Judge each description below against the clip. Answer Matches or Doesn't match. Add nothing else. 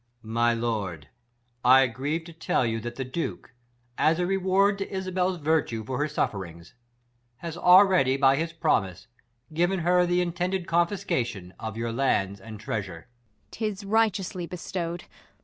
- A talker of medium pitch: Matches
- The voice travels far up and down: Matches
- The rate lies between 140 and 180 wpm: Matches